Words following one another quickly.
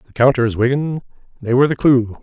No: average, 190 wpm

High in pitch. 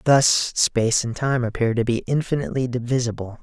No: low, 125 Hz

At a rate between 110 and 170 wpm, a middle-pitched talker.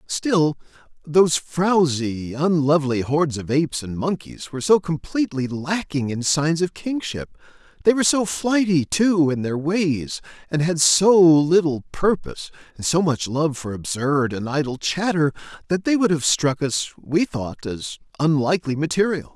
Yes: average, 150 wpm; medium, 155 Hz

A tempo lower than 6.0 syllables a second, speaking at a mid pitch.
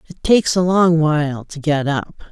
Yes: 4.8 syllables/s; medium, 160 Hz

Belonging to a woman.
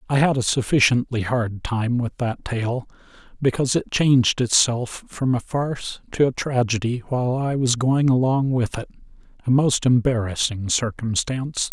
No: male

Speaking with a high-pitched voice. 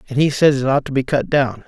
No: low, 135 Hz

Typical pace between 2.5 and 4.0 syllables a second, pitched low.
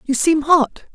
No: 3.9 syllables/s; very high, 295 Hz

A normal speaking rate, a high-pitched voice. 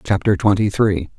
No: average, 150 wpm; low, 100 Hz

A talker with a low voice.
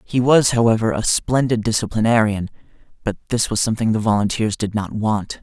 Yes: low, 110 Hz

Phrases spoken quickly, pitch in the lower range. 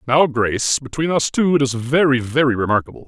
No: average, 195 wpm; low, 130 Hz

